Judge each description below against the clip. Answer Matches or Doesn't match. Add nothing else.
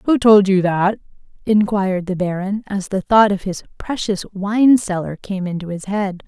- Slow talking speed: Doesn't match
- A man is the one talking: Doesn't match